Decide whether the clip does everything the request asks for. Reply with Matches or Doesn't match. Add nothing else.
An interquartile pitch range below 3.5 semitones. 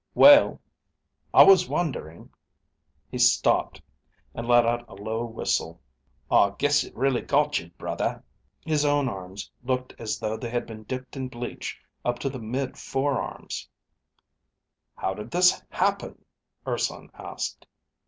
Doesn't match